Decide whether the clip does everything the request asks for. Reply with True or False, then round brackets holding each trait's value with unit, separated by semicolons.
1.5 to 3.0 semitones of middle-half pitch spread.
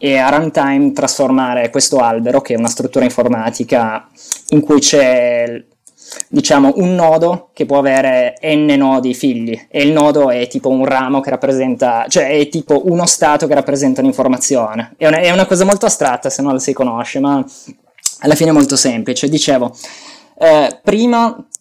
False (3.5 semitones)